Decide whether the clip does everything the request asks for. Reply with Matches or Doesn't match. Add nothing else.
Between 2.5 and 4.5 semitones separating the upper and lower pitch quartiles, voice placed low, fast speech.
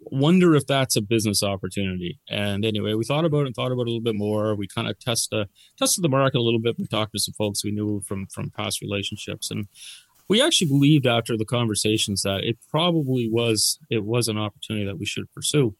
Matches